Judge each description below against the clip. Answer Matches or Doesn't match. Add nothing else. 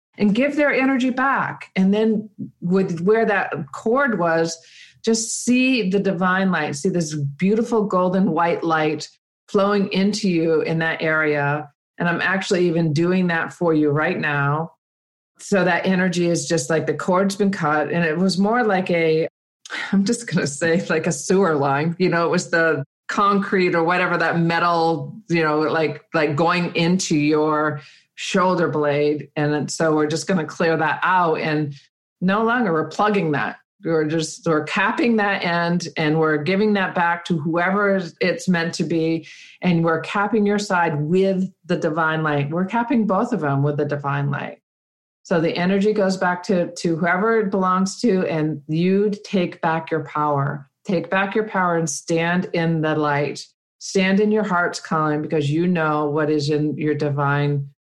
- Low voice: Doesn't match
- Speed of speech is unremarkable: Matches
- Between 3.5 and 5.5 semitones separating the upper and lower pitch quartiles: Matches